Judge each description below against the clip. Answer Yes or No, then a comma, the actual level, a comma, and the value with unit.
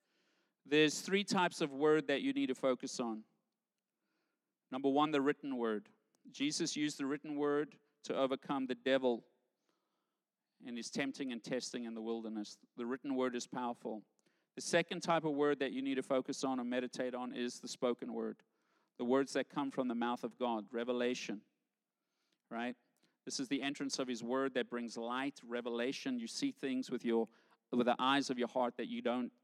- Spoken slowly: No, average, 190 wpm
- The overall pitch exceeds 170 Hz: No, low, 130 Hz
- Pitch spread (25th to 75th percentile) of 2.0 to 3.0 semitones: Yes, average, 2.7 semitones